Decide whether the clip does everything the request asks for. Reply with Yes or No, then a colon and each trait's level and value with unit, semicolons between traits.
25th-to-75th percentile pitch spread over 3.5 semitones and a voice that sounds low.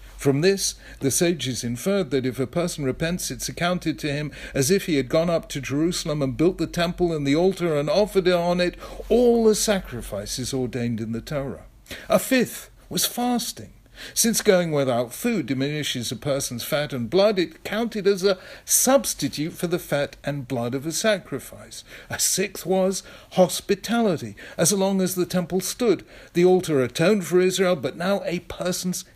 No: wide, 5.6 semitones; medium, 170 Hz